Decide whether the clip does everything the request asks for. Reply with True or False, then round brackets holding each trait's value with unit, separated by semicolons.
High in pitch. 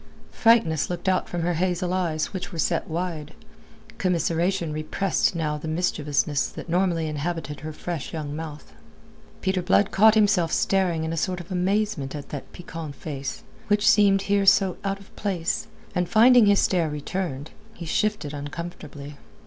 False (175 Hz)